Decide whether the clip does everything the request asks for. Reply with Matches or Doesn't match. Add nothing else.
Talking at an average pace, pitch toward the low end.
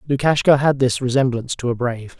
Matches